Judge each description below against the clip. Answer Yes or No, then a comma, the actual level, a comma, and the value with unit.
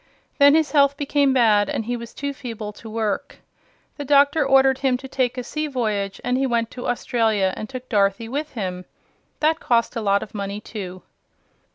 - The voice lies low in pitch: No, high, 245 Hz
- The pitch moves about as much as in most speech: Yes, average, 4.5 semitones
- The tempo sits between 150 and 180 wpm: No, average, 195 wpm